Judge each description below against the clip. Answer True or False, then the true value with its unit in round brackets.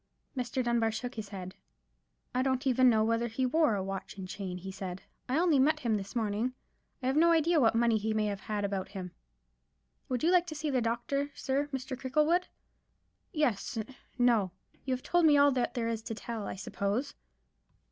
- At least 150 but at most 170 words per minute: False (190 wpm)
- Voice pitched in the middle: False (240 Hz)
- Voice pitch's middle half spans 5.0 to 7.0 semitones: False (4.5 semitones)